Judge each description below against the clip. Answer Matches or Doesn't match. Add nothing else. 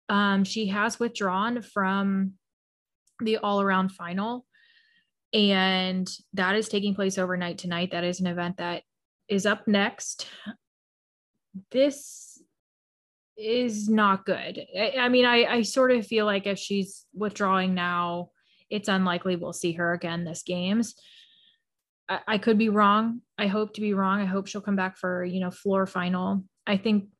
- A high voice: Matches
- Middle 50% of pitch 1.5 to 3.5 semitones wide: Matches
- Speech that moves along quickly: Doesn't match